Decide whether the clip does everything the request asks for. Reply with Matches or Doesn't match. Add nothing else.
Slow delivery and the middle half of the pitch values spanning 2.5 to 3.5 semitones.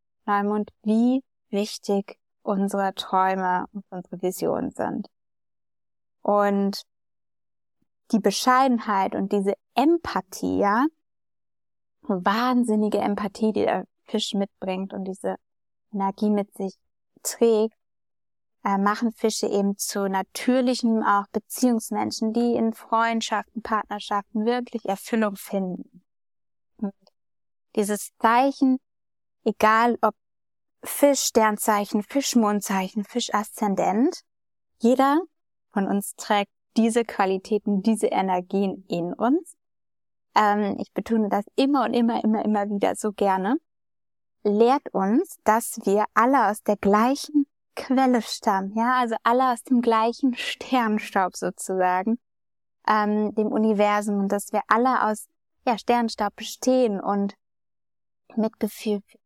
Matches